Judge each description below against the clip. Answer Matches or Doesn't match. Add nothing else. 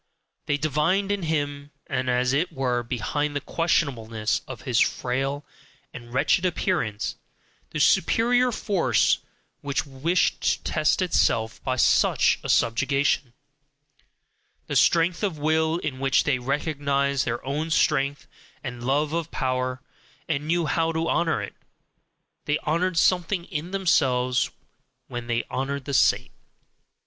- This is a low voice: Doesn't match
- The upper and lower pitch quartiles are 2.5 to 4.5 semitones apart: Matches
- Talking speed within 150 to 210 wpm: Doesn't match